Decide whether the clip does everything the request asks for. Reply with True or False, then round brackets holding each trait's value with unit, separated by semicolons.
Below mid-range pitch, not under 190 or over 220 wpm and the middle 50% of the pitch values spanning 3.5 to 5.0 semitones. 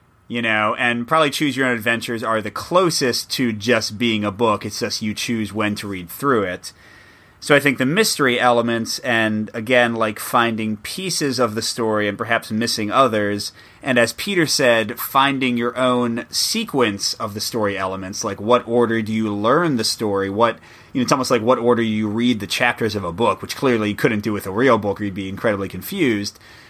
False (115 Hz; 205 wpm; 2.8 semitones)